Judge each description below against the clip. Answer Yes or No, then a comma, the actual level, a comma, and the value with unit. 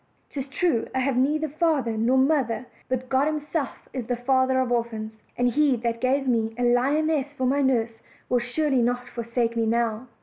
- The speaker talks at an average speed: Yes, average, 190 wpm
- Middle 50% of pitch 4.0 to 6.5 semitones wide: No, average, 2.9 semitones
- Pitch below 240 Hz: No, very high, 255 Hz